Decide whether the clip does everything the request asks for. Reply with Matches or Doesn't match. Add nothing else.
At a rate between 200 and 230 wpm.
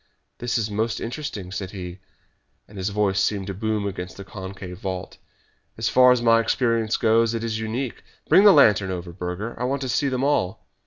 Matches